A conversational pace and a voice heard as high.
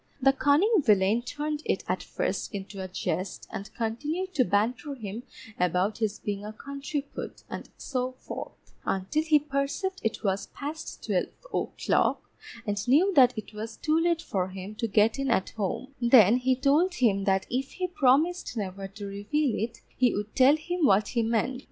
Yes: average, 180 wpm; high, 245 Hz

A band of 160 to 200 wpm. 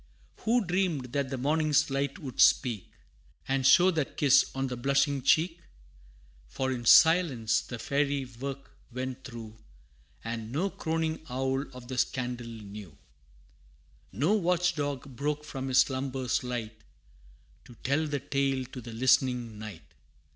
No: average, 140 wpm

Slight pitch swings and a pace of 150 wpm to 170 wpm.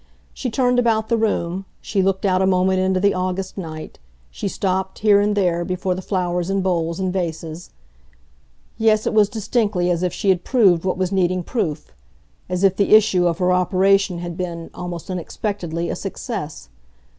No: narrow, 2.3 semitones; average, 180 wpm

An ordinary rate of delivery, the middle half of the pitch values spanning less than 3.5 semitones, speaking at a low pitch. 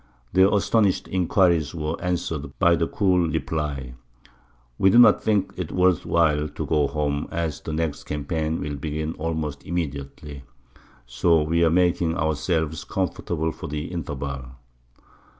Yes: average, 145 wpm; average, 2.8 semitones; very low, 80 Hz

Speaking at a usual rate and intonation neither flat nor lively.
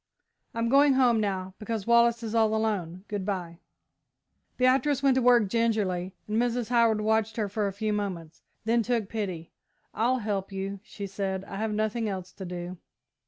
Yes: average, 175 wpm; average, 3.2 semitones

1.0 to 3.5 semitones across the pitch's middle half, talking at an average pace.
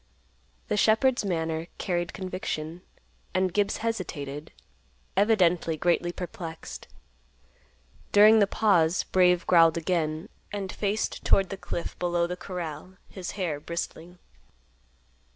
No: average, 3.1 semitones; slow, 110 wpm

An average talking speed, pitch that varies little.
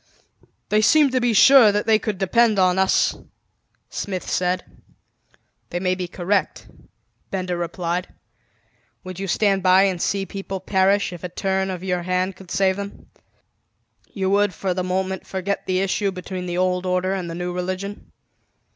Yes: average, 165 wpm; narrow, 1.5 semitones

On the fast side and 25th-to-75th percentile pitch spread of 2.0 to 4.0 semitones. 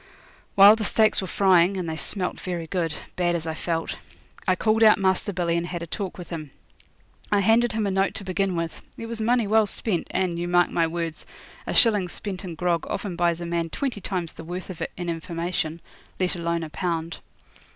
Yes: fast, 215 wpm; average, 2.8 semitones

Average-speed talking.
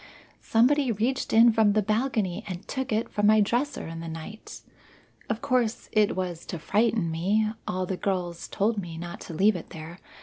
Yes: average, 195 wpm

